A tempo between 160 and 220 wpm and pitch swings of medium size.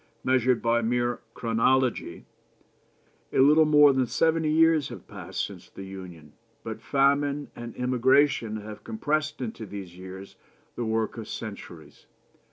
No: slow, 135 wpm; average, 4.5 semitones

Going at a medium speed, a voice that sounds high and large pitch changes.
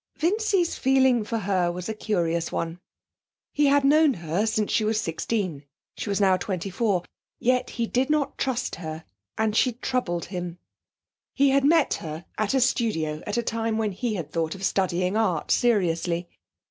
Yes: average, 175 wpm; high, 210 Hz; wide, 6.2 semitones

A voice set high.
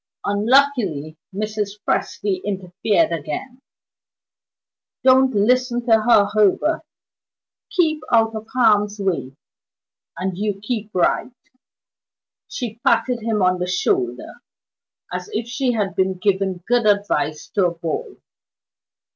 Yes: high, 210 Hz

